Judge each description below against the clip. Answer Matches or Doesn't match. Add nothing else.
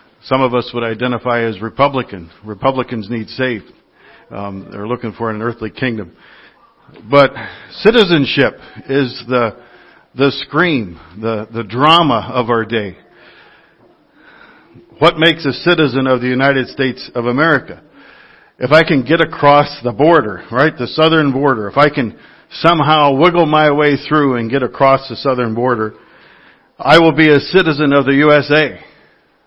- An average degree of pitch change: Matches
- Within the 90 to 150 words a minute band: Matches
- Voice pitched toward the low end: Matches